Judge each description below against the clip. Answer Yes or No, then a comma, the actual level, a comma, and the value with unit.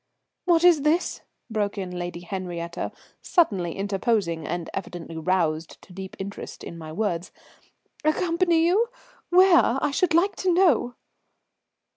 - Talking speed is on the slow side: Yes, slow, 130 wpm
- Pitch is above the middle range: Yes, high, 200 Hz